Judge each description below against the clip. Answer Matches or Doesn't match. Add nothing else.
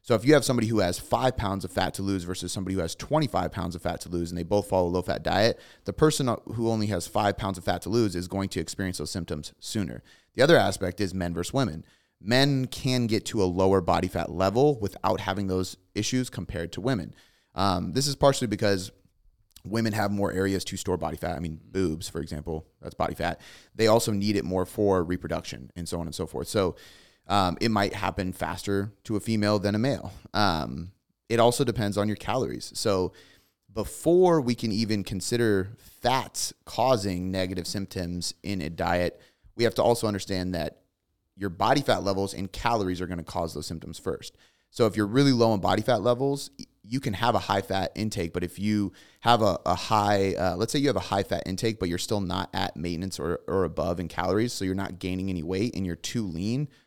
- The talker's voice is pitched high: Doesn't match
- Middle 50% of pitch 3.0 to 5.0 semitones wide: Matches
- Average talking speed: Doesn't match